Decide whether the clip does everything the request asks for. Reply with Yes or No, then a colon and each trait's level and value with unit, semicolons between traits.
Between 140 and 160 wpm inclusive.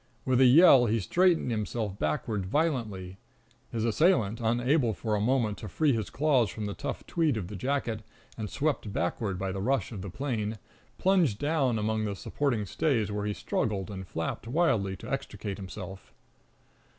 No: average, 175 wpm